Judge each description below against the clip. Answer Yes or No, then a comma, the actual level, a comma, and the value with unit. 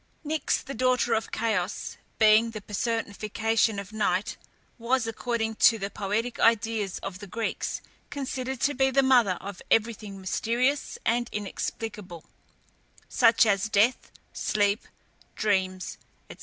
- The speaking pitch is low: No, high, 220 Hz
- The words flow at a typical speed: No, slow, 130 wpm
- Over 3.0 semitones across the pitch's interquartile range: No, average, 2.7 semitones